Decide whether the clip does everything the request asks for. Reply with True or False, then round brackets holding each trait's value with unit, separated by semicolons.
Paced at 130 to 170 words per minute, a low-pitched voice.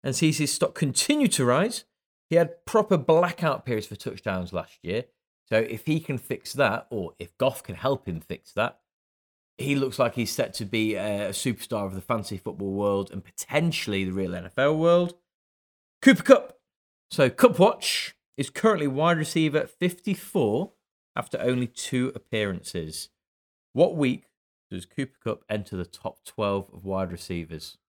True (165 wpm; 120 Hz)